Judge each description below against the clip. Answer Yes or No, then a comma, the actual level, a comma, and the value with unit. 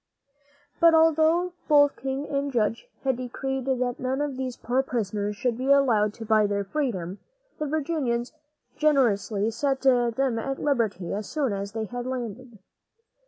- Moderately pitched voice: No, very high, 255 Hz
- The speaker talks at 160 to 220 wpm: No, average, 150 wpm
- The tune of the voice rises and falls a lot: No, average, 4.0 semitones